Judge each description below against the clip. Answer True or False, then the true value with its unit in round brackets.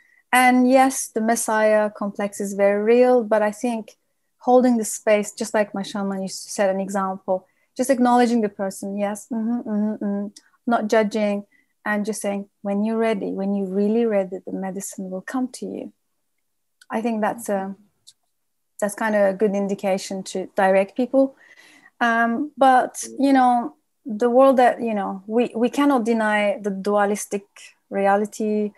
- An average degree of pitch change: True (3.5 semitones)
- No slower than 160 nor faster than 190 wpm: True (165 wpm)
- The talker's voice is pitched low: False (215 Hz)